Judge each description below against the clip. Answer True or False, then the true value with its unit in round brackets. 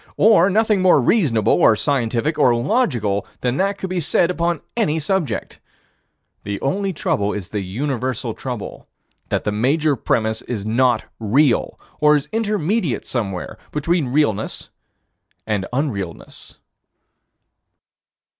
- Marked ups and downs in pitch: True (7.6 semitones)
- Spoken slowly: True (125 wpm)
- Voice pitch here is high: False (135 Hz)